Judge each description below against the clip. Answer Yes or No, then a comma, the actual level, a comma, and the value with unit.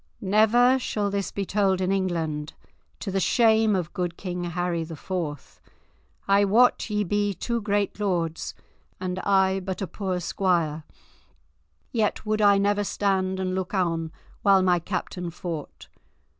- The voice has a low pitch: No, high, 190 Hz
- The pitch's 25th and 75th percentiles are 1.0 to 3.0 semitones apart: Yes, narrow, 2.6 semitones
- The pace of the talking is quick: No, average, 150 wpm